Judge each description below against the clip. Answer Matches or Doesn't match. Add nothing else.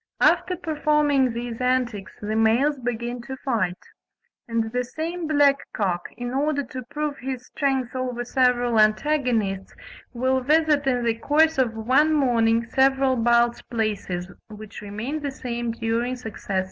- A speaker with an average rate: Matches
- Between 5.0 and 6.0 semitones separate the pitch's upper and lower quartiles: Doesn't match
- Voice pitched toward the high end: Matches